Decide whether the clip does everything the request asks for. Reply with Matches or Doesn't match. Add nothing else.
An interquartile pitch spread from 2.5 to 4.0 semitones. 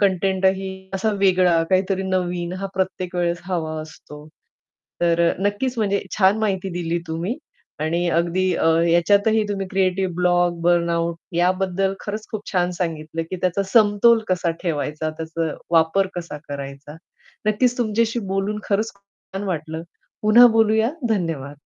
Matches